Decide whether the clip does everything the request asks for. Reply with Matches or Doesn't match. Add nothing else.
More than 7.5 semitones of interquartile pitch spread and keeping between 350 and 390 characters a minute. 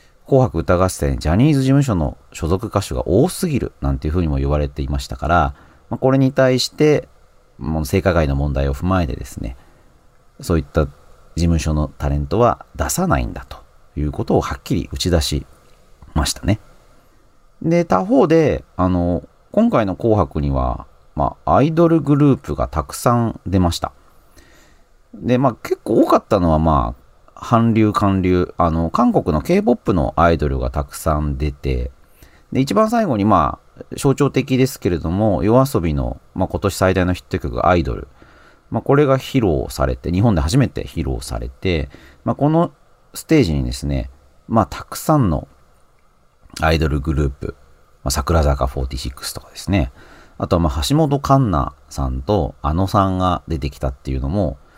Doesn't match